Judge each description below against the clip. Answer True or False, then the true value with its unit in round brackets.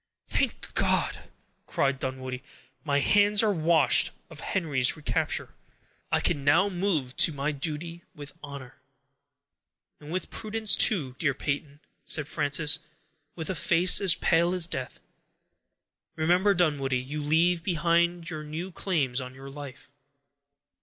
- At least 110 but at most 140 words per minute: True (135 wpm)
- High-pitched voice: False (155 Hz)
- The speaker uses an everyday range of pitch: True (3.8 semitones)